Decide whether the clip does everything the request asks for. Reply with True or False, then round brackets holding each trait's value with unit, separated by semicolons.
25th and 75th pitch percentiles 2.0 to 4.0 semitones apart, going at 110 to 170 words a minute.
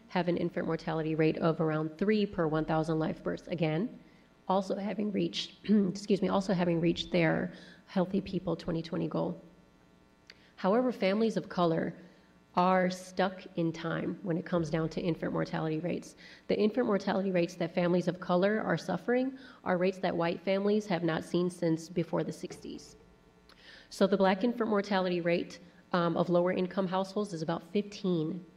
True (2.7 semitones; 165 wpm)